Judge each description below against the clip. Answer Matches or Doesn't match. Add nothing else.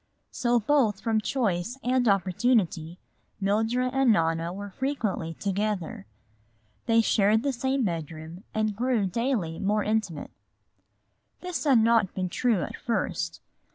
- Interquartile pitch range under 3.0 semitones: Doesn't match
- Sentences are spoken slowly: Matches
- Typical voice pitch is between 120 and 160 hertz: Doesn't match